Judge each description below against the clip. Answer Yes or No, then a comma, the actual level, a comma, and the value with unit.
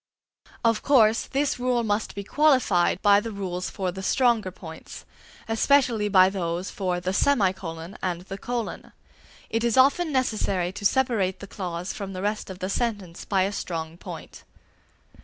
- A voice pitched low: No, high, 200 Hz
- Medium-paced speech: Yes, average, 160 wpm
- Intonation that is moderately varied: Yes, average, 4.1 semitones